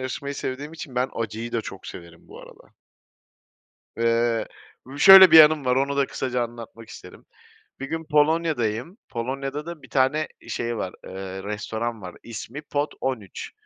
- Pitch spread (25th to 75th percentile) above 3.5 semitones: Yes, average, 4.3 semitones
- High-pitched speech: No, low, 130 Hz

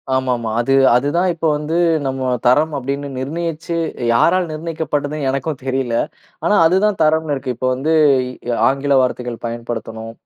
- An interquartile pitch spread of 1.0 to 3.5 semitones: No, average, 3.9 semitones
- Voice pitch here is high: No, medium, 140 Hz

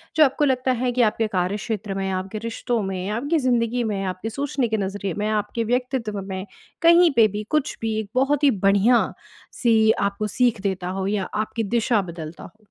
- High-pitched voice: Yes, high, 220 Hz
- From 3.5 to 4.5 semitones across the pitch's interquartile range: Yes, average, 4.1 semitones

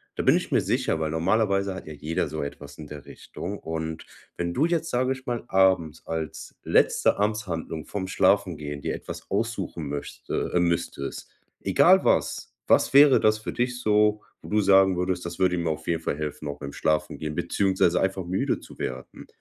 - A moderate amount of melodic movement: Yes, average, 4.8 semitones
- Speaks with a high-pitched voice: No, very low, 90 Hz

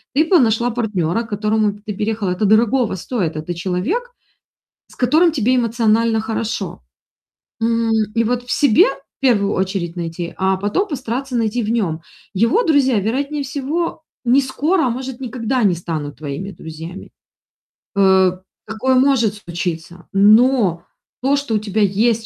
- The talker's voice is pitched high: Yes, high, 220 Hz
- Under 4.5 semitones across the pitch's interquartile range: No, average, 5.0 semitones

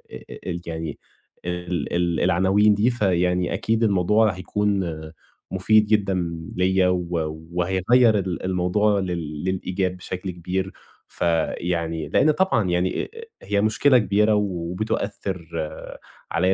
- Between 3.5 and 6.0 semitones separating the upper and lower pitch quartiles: No, average, 2.8 semitones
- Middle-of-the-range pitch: No, very low, 95 Hz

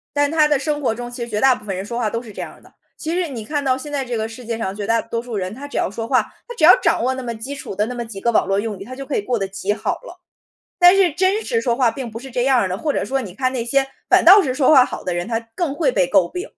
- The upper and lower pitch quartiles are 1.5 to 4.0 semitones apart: No, average, 4.4 semitones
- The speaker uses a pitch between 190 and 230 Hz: No, high, 245 Hz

